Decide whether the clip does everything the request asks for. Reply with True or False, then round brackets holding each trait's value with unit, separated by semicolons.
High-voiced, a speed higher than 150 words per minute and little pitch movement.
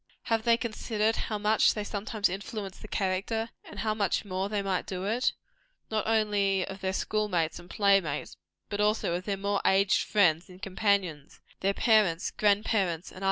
True (200 Hz; 190 wpm; 2.3 semitones)